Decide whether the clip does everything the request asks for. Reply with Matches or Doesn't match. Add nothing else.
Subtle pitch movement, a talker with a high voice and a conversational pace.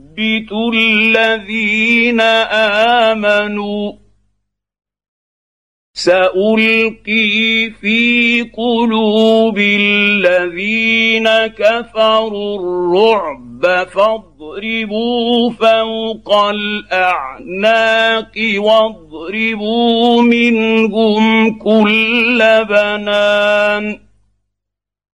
Doesn't match